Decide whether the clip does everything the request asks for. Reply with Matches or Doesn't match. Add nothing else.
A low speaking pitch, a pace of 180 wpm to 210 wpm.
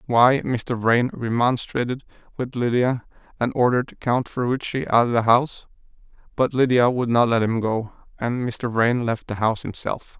Doesn't match